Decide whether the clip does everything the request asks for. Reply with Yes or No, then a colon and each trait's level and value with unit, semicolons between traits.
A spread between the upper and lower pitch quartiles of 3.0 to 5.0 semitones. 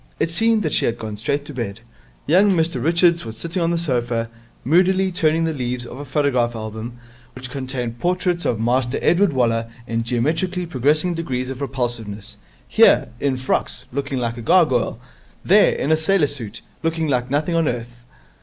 No: wide, 5.6 semitones